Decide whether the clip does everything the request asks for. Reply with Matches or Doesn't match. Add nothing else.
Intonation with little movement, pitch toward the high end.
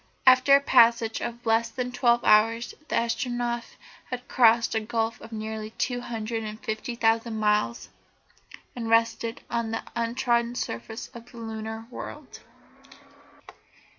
Matches